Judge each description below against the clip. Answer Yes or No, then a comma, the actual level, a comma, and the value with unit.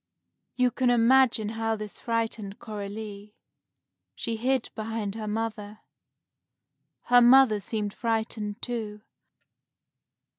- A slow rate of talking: Yes, slow, 100 wpm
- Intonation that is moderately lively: No, narrow, 2.0 semitones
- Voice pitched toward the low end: No, high, 220 Hz